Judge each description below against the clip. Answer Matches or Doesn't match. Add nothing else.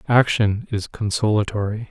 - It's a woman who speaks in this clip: Doesn't match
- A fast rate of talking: Doesn't match